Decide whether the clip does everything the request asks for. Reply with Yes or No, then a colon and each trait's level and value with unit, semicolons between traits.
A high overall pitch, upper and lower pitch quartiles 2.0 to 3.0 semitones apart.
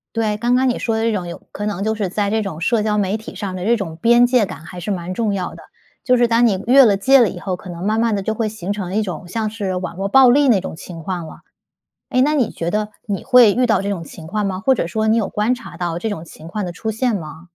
No: high, 210 Hz; average, 3.8 semitones